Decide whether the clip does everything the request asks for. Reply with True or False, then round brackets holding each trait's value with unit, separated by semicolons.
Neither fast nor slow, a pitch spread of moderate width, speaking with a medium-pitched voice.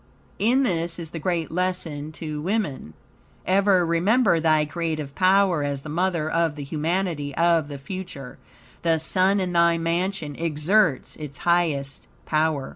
True (145 wpm; 3.5 semitones; 165 Hz)